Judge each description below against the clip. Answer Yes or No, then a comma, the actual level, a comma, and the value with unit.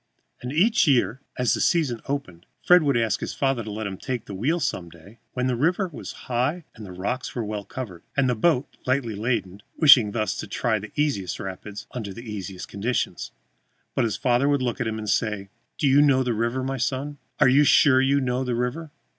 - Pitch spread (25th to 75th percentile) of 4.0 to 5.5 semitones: Yes, average, 4.5 semitones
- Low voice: Yes, low, 125 Hz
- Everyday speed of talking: No, fast, 215 wpm